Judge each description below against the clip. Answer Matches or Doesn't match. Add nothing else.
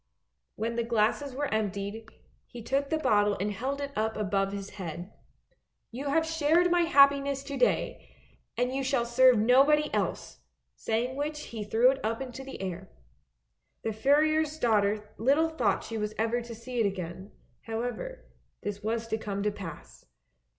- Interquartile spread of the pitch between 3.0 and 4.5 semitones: Doesn't match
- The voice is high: Matches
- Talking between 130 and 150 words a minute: Doesn't match